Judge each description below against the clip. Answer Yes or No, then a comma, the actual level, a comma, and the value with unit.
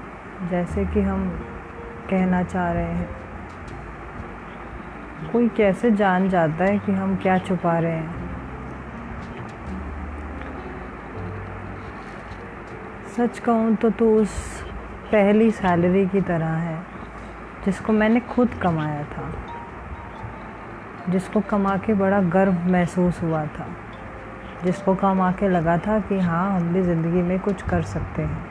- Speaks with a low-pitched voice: No, medium, 180 Hz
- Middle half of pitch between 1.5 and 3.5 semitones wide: No, average, 4.5 semitones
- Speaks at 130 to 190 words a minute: No, average, 120 wpm